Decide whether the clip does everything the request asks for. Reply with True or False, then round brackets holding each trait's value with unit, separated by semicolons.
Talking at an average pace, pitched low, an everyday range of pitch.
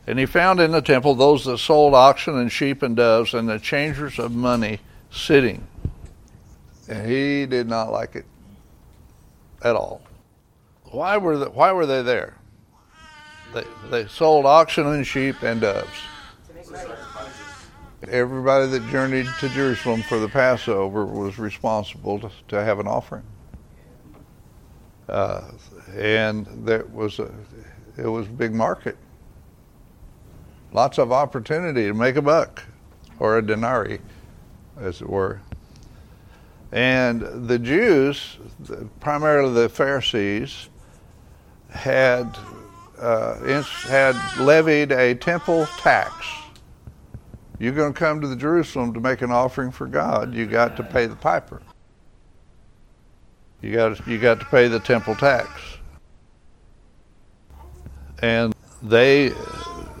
False (125 wpm; 120 Hz; 4.2 semitones)